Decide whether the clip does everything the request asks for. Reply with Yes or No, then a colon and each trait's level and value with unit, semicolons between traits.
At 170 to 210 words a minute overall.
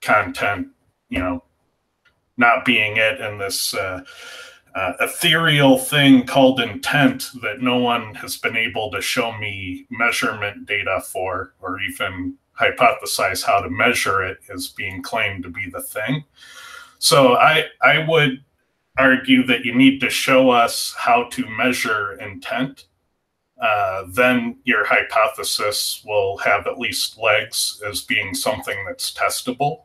No: average, 140 wpm